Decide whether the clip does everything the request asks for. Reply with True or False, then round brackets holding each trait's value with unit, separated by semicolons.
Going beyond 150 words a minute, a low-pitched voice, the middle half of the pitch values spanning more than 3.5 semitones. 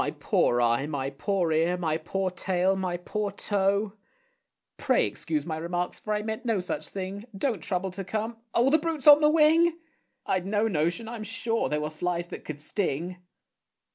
False (185 wpm; 190 Hz; 4.5 semitones)